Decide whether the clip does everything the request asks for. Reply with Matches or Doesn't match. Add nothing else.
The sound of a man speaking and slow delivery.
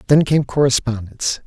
Matches